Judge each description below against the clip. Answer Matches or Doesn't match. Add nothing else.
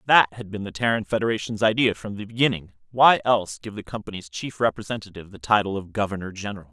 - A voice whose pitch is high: Doesn't match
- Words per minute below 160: Doesn't match